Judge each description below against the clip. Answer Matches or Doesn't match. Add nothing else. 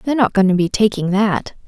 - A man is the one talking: Doesn't match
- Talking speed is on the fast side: Matches